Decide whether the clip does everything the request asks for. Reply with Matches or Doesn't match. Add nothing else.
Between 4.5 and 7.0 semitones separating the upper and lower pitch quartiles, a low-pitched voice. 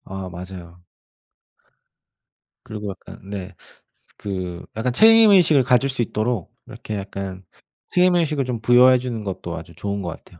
Matches